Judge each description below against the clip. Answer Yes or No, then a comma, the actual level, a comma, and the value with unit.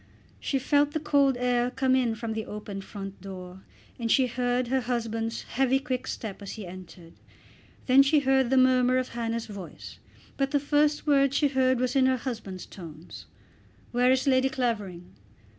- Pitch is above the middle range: Yes, very high, 250 Hz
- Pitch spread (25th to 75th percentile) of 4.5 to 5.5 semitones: No, average, 3.5 semitones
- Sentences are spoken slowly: No, average, 175 wpm